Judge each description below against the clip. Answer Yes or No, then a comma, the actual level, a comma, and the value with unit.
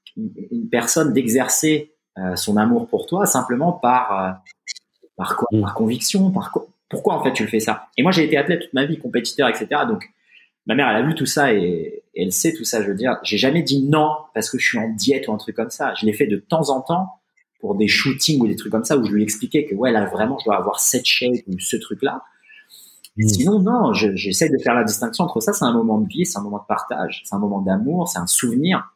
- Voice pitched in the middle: No, low, 130 Hz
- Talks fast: Yes, fast, 255 wpm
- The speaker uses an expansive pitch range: Yes, wide, 8.9 semitones